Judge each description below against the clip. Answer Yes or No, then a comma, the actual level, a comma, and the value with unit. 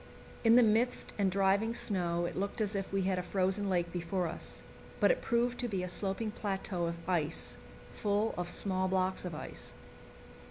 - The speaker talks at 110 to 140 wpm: No, average, 190 wpm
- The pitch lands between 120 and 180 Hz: No, high, 190 Hz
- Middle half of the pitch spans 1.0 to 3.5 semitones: Yes, average, 2.8 semitones